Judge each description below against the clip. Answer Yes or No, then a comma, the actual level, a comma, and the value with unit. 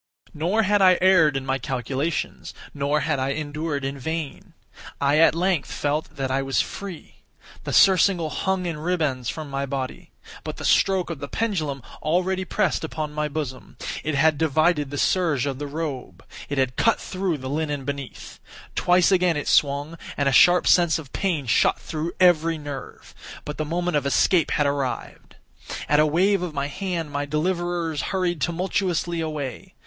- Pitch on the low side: No, medium, 155 Hz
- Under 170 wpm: No, average, 175 wpm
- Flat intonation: No, average, 3.8 semitones